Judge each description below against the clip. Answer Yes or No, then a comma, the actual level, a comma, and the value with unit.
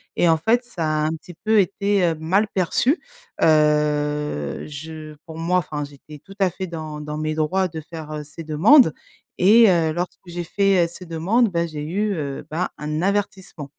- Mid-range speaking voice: Yes, medium, 165 Hz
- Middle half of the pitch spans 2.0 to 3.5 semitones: No, average, 3.9 semitones